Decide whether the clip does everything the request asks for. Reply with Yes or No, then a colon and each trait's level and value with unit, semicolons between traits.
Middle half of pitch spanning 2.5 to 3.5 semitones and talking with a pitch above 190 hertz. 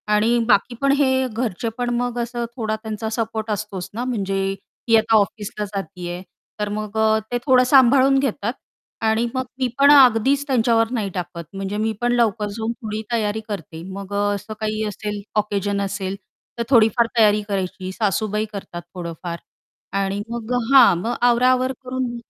Yes: average, 3.0 semitones; high, 220 Hz